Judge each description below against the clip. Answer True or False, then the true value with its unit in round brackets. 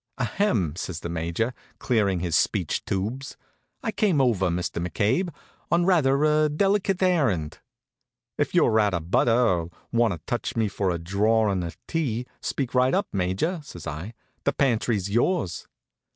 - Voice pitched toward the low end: True (110 Hz)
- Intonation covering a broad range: True (8.0 semitones)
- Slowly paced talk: False (155 wpm)